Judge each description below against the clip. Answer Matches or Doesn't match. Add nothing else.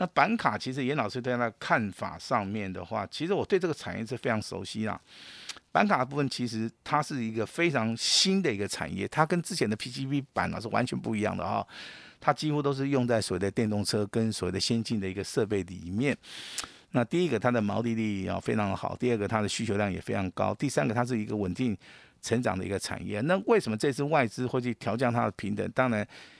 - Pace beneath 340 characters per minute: Doesn't match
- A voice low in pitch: Matches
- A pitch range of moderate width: Matches